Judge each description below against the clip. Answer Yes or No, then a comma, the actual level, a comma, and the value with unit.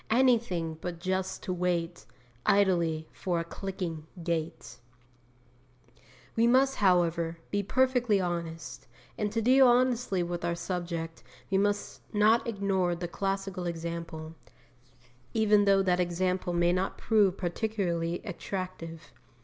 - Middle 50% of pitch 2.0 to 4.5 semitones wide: Yes, average, 3.3 semitones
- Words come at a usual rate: No, slow, 120 wpm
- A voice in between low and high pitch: Yes, medium, 180 Hz